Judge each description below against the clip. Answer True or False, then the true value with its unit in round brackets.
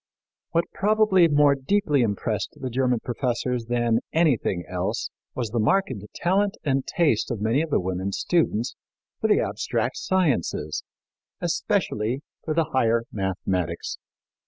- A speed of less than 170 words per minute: True (135 wpm)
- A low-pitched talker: True (130 Hz)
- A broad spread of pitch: True (6.5 semitones)